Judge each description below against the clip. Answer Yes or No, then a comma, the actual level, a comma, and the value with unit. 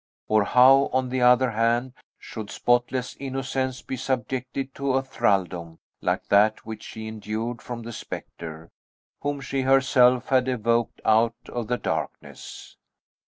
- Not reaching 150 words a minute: Yes, average, 140 wpm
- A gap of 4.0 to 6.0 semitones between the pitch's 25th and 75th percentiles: No, average, 2.9 semitones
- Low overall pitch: Yes, low, 125 Hz